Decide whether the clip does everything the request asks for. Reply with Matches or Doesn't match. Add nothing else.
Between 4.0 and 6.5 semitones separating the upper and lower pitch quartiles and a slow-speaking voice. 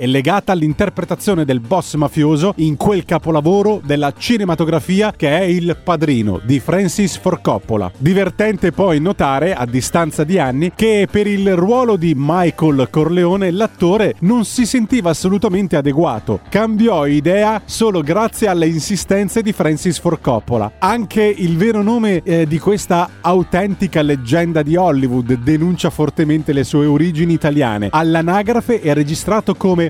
Doesn't match